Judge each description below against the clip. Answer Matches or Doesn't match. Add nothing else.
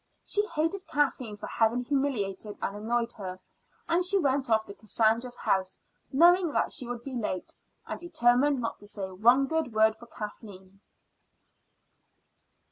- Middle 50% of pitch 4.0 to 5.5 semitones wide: Matches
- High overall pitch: Matches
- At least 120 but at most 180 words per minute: Matches